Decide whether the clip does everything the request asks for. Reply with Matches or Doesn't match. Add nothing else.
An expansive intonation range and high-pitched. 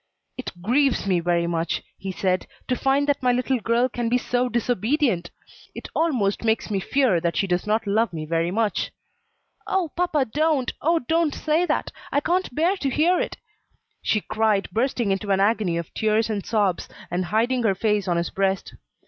Matches